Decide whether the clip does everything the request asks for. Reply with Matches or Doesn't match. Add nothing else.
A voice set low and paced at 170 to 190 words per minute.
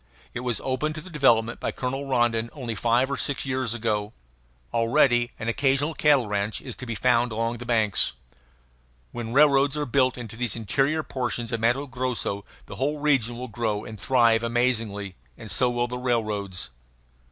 Matches